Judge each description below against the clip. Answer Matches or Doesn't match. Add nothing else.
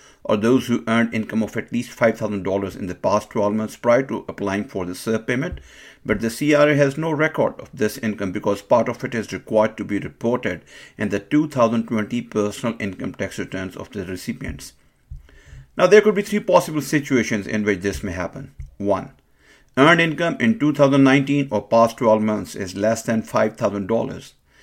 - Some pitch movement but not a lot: Matches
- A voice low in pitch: Matches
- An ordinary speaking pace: Matches